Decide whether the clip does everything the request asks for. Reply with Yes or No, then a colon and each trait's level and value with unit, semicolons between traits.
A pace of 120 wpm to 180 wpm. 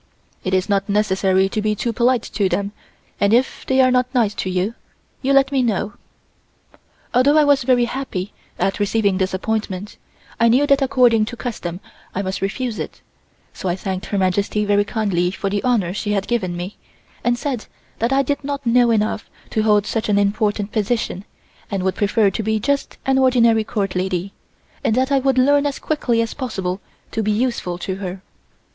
No: average, 195 wpm